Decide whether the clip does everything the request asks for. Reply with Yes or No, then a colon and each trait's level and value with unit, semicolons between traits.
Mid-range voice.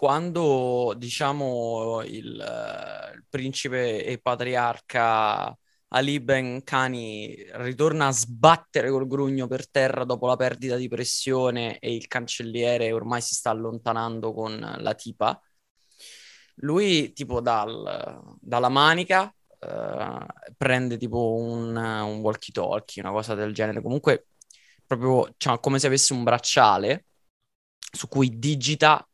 No: low, 125 Hz